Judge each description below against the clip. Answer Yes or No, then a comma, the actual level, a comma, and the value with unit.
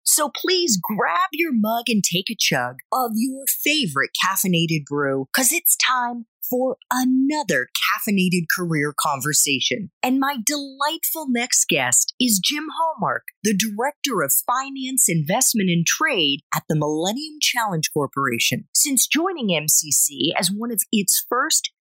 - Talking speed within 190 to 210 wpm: No, average, 140 wpm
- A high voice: Yes, high, 225 Hz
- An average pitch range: No, wide, 8.5 semitones